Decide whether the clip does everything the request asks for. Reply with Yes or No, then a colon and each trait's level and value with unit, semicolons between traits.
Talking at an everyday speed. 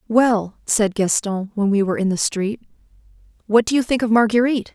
Yes: average, 190 wpm